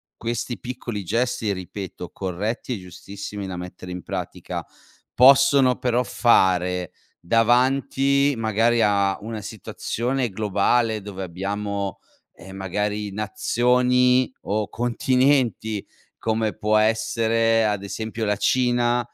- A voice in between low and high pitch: No, low, 110 Hz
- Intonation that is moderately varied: Yes, average, 3.5 semitones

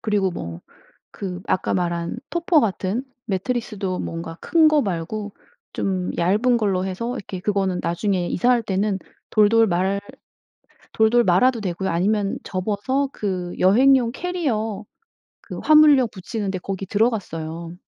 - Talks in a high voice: Yes, high, 200 Hz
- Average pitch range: Yes, average, 4.2 semitones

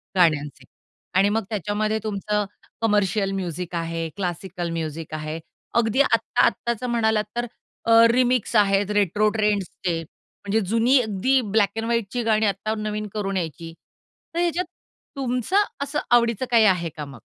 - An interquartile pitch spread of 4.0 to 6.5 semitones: Yes, average, 4.4 semitones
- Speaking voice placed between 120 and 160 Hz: No, high, 210 Hz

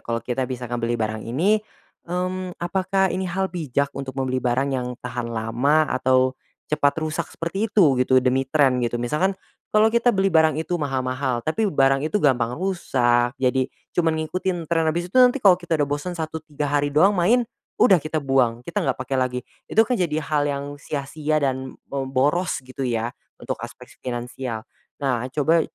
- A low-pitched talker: No, medium, 145 Hz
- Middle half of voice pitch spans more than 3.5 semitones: Yes, average, 5.2 semitones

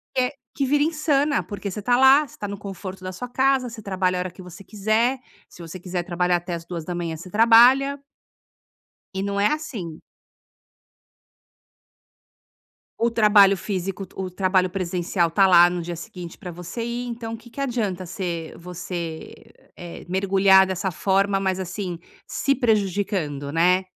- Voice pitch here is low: No, high, 190 Hz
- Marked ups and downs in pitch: No, average, 4.3 semitones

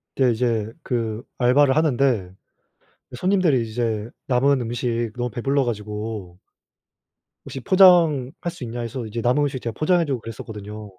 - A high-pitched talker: No, low, 120 Hz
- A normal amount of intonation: Yes, average, 3.7 semitones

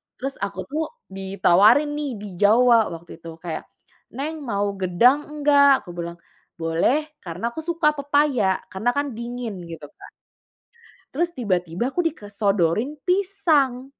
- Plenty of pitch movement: Yes, wide, 7.3 semitones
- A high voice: Yes, high, 235 Hz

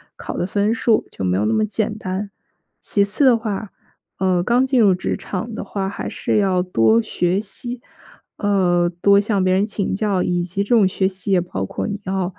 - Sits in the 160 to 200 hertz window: Yes, high, 195 Hz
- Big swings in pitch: No, narrow, 2.6 semitones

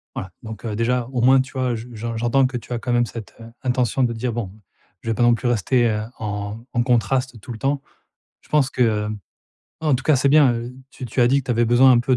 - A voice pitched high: No, low, 120 Hz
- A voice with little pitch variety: Yes, narrow, 2.2 semitones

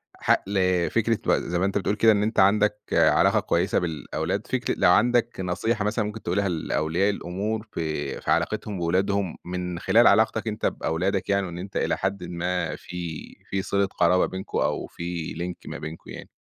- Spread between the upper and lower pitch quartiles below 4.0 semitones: Yes, average, 3.0 semitones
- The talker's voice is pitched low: Yes, very low, 95 Hz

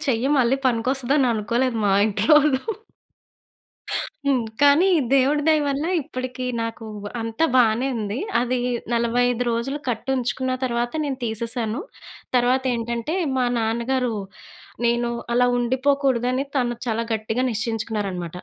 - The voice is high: Yes, high, 245 Hz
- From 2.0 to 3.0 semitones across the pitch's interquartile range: Yes, narrow, 2.5 semitones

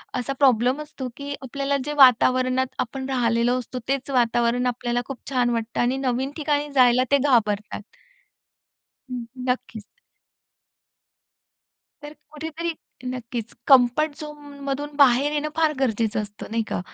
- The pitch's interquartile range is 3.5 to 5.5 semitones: No, average, 2.9 semitones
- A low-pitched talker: No, very high, 255 Hz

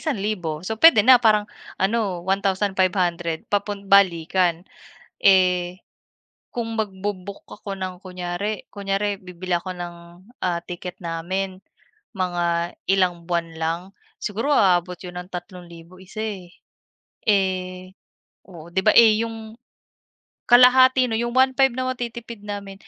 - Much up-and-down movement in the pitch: No, average, 3.3 semitones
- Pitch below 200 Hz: Yes, high, 190 Hz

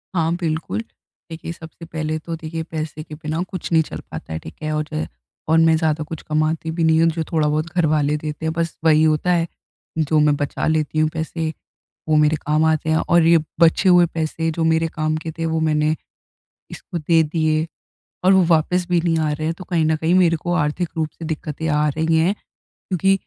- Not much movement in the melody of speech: Yes, narrow, 1.2 semitones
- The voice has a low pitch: No, medium, 160 Hz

